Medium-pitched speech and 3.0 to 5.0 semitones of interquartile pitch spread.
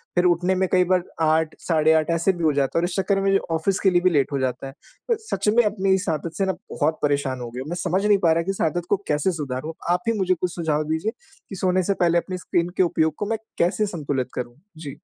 Yes: medium, 170 Hz; average, 3.5 semitones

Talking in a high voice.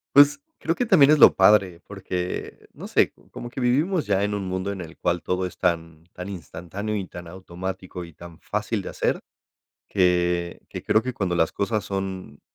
No: very low, 95 Hz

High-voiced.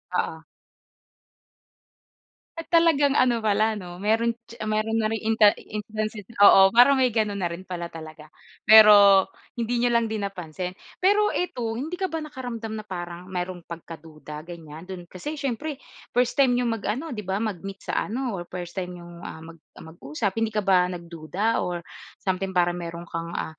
Yes: high, 205 Hz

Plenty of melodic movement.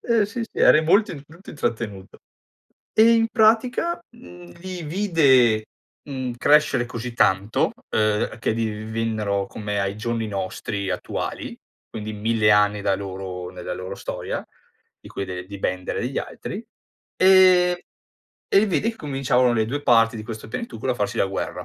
Yes: wide, 8.2 semitones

